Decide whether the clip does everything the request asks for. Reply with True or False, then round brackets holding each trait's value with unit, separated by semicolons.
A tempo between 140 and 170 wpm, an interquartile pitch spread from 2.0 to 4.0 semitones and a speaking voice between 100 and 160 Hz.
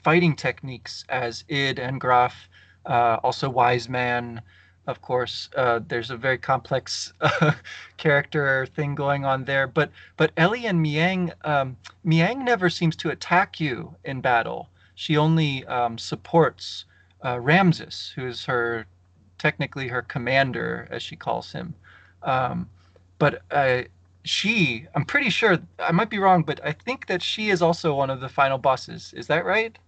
False (160 wpm; 5.2 semitones; 135 Hz)